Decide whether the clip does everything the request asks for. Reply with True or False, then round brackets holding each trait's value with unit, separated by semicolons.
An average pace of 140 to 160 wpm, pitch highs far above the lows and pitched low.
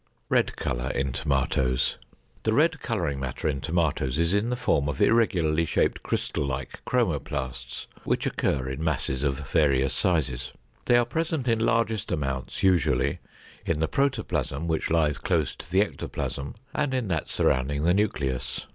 True (155 wpm; 7.7 semitones; 80 Hz)